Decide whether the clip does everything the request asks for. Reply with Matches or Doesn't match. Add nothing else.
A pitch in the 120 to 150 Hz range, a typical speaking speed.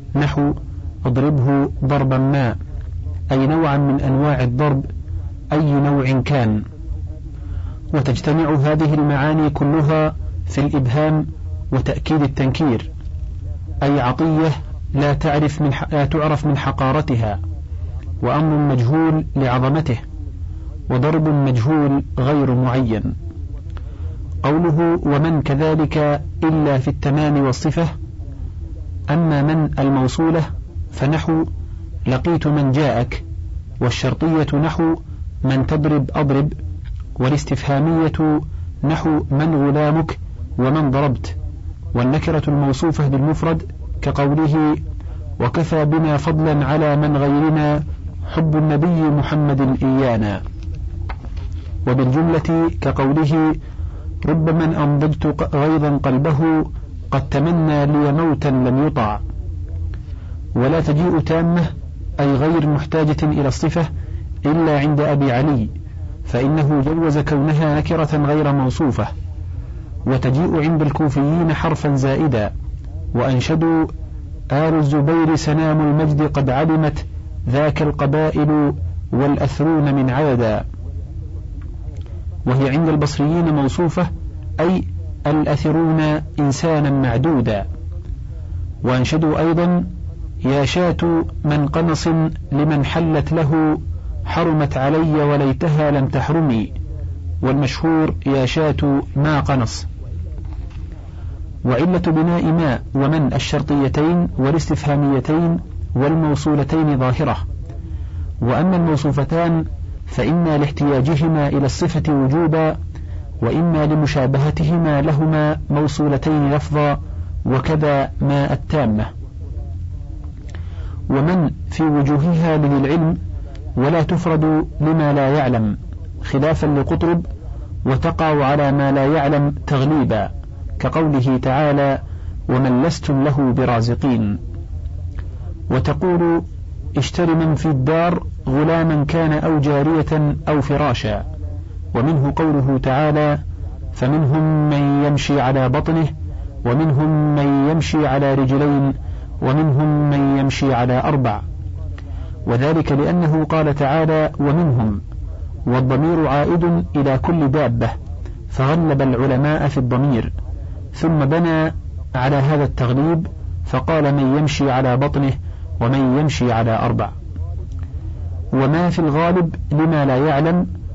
Matches